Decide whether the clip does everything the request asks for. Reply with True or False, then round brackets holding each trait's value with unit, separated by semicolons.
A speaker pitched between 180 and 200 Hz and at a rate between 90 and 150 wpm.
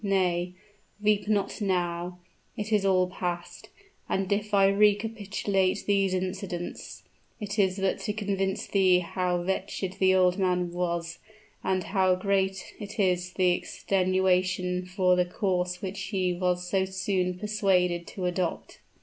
True (185 Hz; 135 wpm)